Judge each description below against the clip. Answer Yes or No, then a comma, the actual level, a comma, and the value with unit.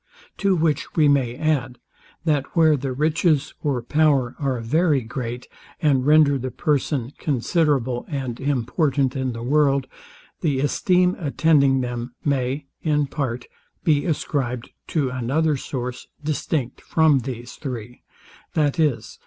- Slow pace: Yes, slow, 130 wpm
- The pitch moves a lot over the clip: No, average, 3.4 semitones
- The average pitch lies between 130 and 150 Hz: Yes, medium, 140 Hz